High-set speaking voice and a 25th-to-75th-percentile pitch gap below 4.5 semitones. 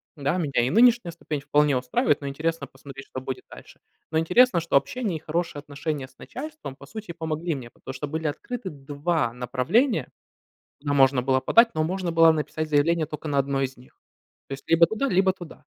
No: medium, 155 Hz; average, 3.9 semitones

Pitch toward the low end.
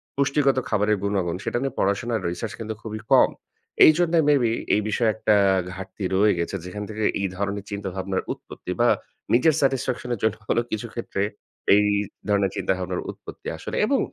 Yes: low, 105 Hz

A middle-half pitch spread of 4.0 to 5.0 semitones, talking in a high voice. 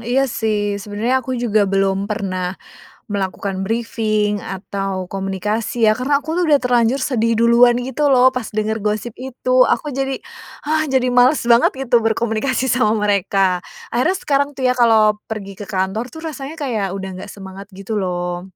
Yes: average, 4.3 semitones; high, 220 Hz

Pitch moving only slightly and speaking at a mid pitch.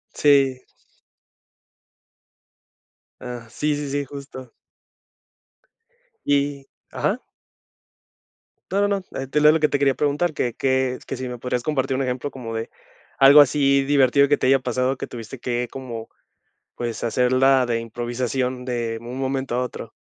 No: narrow, 2.2 semitones; low, 130 Hz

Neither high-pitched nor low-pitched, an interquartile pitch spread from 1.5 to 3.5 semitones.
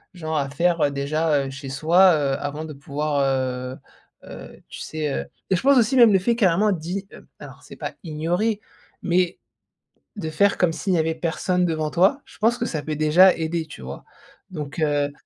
No: medium, 160 Hz; average, 4.0 semitones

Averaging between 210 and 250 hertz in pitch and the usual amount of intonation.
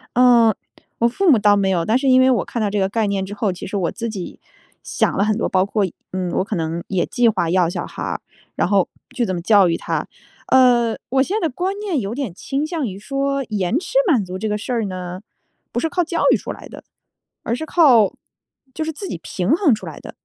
No: high, 220 Hz; wide, 5.7 semitones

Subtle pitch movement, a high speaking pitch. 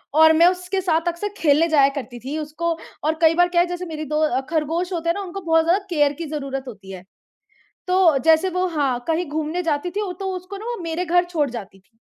No: average, 3.2 semitones; very high, 325 Hz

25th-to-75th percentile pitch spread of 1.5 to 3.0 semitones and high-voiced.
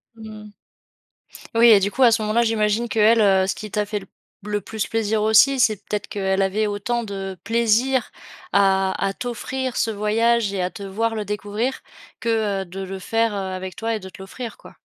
Yes: narrow, 2.5 semitones; high, 215 Hz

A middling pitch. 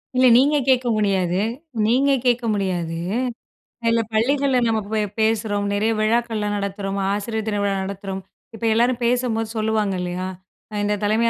No: high, 220 Hz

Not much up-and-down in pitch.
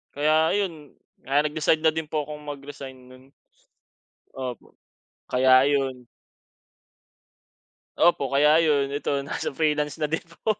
Yes: narrow, 2.3 semitones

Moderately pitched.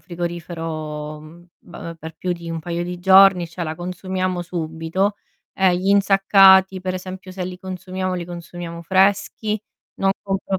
Yes: medium, 180 Hz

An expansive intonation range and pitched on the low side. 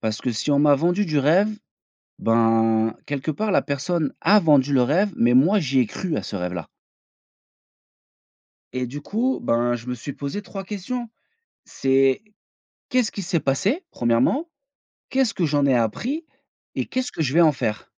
No: wide, 8.0 semitones; medium, 145 Hz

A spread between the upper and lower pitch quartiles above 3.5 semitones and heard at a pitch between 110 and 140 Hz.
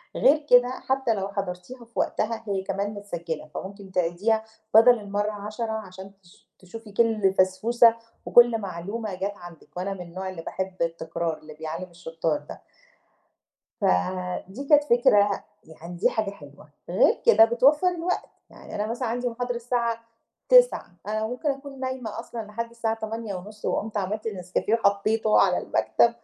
No: average, 4.0 semitones; high, 210 Hz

